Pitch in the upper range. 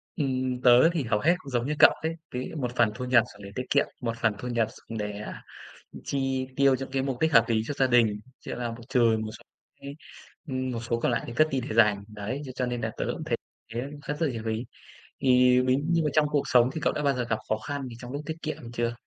No: low, 125 Hz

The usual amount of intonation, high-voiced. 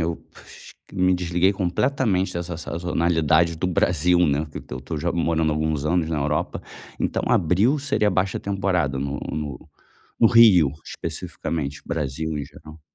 No: average, 3.1 semitones; very low, 85 Hz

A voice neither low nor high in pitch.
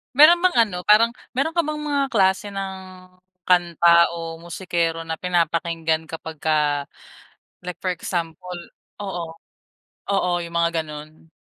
Yes: medium, 175 Hz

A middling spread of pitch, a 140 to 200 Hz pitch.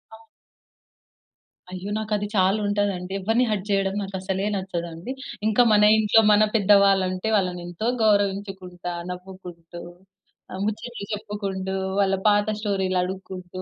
No: narrow, 1.9 semitones; high, 195 Hz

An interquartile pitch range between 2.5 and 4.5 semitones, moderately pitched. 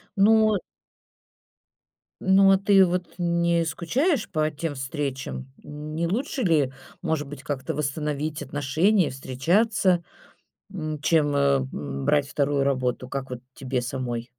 No: average, 5.0 semitones; medium, 150 Hz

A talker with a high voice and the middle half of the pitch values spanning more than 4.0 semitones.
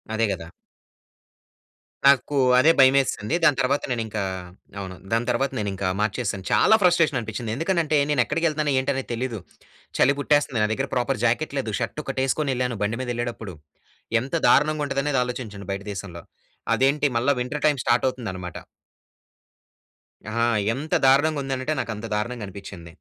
No: low, 130 Hz; average, 4.4 semitones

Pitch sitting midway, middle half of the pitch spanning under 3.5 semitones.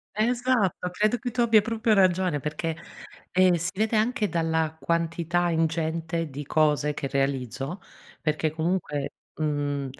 No: medium, 165 Hz; average, 4.6 semitones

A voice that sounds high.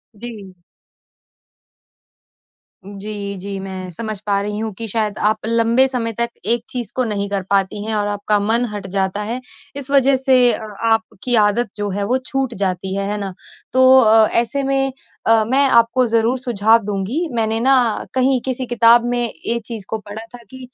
Yes: high, 225 Hz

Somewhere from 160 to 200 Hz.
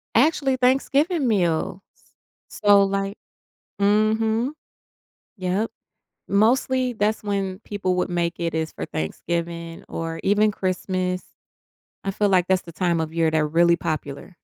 Yes: high, 190 Hz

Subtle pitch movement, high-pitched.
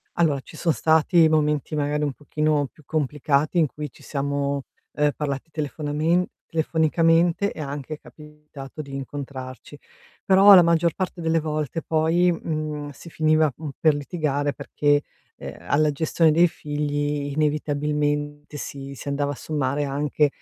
No: narrow, 1.7 semitones; medium, 150 Hz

